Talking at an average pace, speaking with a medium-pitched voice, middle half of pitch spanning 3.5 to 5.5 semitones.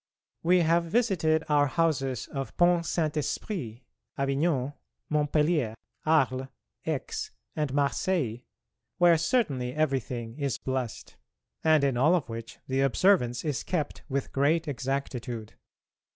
No: slow, 120 wpm; medium, 145 Hz; average, 4.1 semitones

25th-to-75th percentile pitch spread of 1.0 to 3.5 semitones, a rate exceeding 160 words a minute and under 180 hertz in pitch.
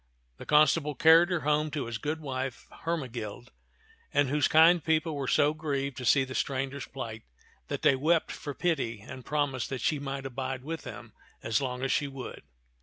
Yes: average, 2.8 semitones; average, 185 wpm; medium, 140 Hz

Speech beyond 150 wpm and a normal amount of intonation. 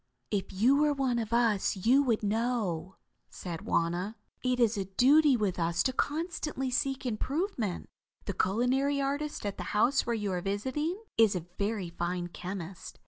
No: average, 165 wpm; wide, 5.9 semitones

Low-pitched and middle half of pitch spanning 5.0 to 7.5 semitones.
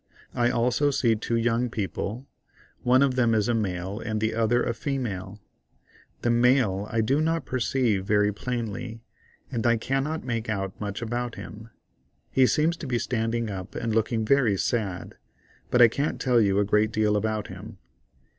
No: low, 115 Hz; average, 2.8 semitones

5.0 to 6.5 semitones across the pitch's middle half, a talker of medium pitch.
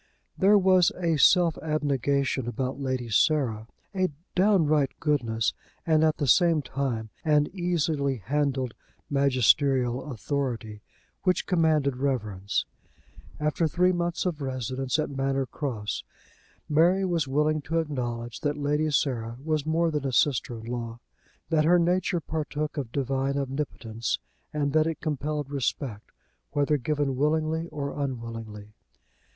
No: average, 3.5 semitones; medium, 145 Hz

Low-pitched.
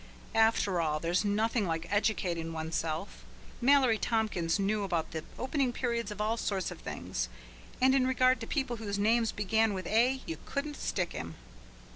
No: high, 210 Hz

